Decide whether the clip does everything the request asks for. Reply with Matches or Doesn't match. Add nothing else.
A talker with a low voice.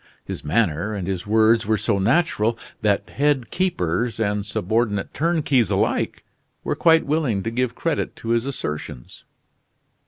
Matches